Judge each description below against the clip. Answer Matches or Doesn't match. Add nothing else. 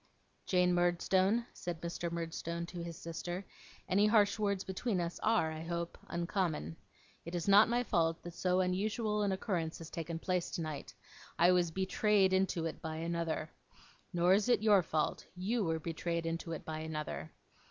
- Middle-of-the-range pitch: Matches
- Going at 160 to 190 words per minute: Matches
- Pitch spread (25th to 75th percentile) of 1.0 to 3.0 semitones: Matches